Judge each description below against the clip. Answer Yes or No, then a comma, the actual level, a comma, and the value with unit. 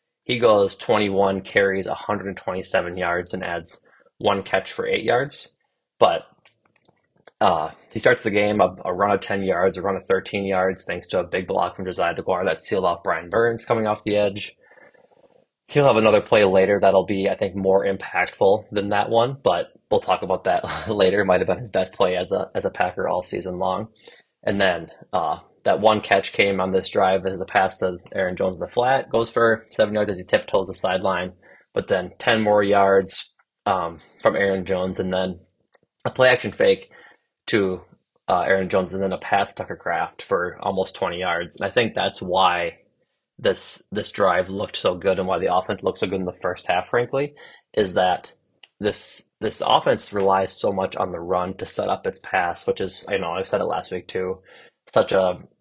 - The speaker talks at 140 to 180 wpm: No, fast, 205 wpm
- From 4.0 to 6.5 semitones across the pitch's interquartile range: No, average, 3.6 semitones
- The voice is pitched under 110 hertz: Yes, low, 100 Hz